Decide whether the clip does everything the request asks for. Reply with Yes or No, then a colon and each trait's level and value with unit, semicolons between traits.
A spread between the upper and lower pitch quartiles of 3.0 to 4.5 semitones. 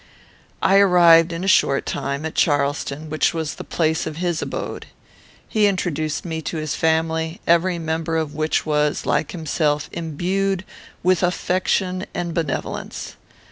No: narrow, 2.4 semitones